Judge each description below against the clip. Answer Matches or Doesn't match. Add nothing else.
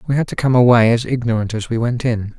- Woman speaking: Doesn't match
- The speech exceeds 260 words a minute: Matches